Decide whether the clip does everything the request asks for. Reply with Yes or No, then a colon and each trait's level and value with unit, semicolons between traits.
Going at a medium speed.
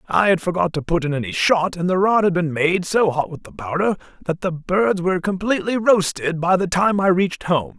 No: fast, 240 wpm